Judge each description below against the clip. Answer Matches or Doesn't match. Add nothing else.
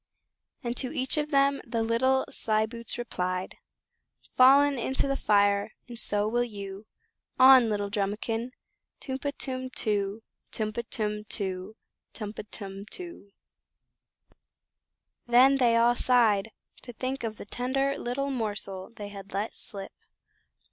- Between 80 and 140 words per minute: Matches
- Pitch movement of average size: Matches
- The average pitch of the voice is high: Matches